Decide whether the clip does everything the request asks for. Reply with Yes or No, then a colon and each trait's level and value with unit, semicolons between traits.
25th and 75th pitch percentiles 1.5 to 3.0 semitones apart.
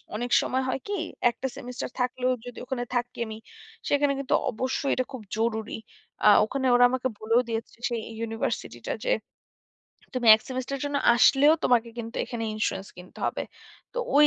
Yes: narrow, 2.4 semitones